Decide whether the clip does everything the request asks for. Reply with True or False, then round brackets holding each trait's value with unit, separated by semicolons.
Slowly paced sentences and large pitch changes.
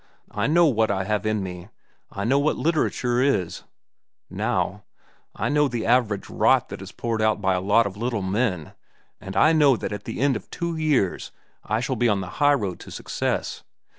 False (195 wpm; 5.9 semitones)